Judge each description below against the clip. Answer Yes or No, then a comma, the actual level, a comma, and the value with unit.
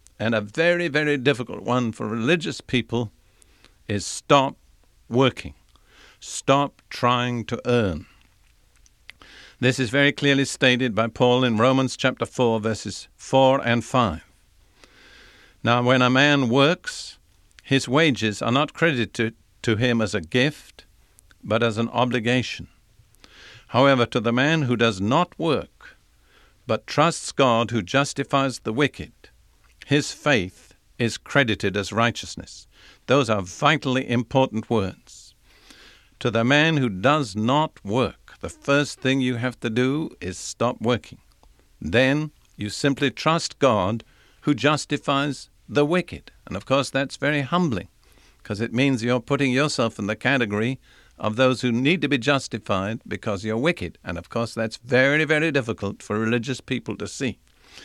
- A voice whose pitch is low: Yes, low, 125 Hz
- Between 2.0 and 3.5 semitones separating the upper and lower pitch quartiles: No, average, 4.1 semitones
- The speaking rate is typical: Yes, average, 145 wpm